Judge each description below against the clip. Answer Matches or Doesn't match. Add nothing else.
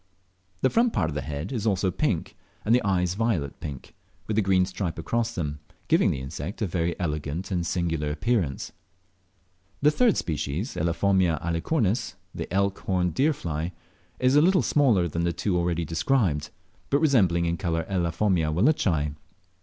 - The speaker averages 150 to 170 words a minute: Matches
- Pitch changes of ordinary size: Matches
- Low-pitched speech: Matches